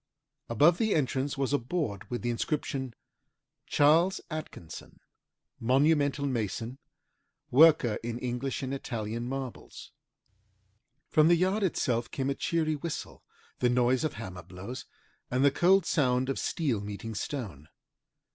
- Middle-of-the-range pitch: No, low, 130 Hz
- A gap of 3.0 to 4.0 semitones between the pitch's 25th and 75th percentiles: No, average, 4.4 semitones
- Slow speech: Yes, slow, 130 wpm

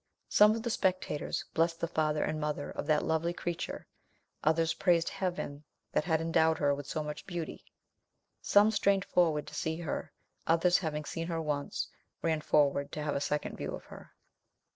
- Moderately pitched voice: Yes, medium, 160 Hz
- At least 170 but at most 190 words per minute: Yes, average, 180 wpm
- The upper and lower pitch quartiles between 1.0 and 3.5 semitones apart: Yes, narrow, 2.5 semitones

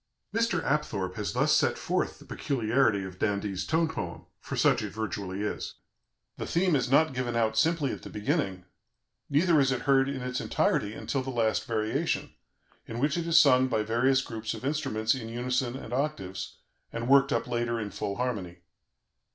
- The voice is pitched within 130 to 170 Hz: No, low, 120 Hz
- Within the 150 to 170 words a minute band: No, average, 185 wpm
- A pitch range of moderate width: Yes, average, 4.3 semitones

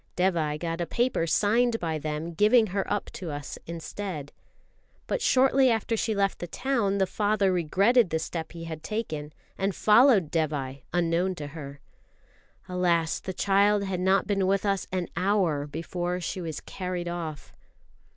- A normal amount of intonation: Yes, average, 3.9 semitones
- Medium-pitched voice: Yes, medium, 180 Hz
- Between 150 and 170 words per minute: Yes, average, 160 wpm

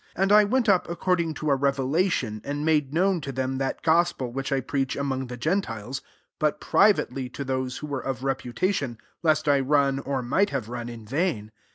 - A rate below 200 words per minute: No, fast, 205 wpm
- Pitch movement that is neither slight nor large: Yes, average, 4.0 semitones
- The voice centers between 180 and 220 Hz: No, medium, 140 Hz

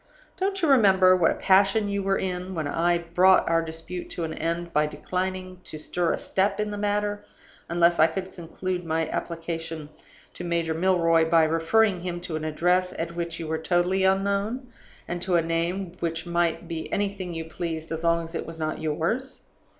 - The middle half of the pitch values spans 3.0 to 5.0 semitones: No, narrow, 2.5 semitones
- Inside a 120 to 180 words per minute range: No, average, 195 wpm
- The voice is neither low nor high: Yes, medium, 175 Hz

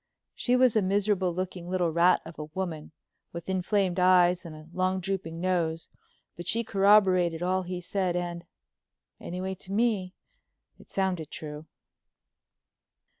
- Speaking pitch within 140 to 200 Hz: Yes, medium, 185 Hz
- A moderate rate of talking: No, slow, 130 wpm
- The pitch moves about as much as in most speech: No, narrow, 2.0 semitones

